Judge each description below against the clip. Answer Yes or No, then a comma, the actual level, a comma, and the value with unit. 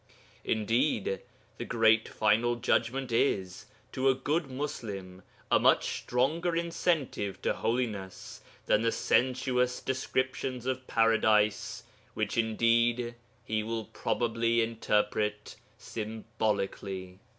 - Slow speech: Yes, slow, 100 wpm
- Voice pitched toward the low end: Yes, low, 115 Hz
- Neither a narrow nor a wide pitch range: Yes, average, 3.2 semitones